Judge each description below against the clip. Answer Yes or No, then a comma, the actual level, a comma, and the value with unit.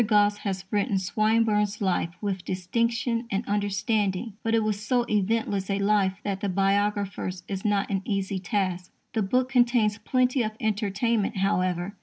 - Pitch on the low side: No, high, 205 Hz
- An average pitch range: No, narrow, 2.3 semitones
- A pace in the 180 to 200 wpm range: No, average, 155 wpm